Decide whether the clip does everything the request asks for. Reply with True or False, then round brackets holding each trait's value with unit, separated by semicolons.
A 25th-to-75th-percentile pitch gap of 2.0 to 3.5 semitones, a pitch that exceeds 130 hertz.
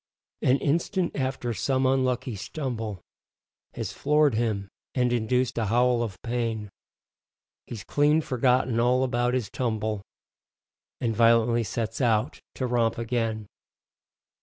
False (2.4 semitones; 120 Hz)